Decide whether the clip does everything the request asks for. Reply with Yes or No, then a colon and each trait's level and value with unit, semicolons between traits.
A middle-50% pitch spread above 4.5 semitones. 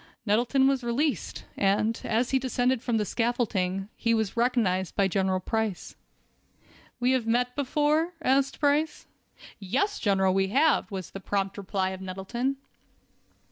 Yes: average, 5.2 semitones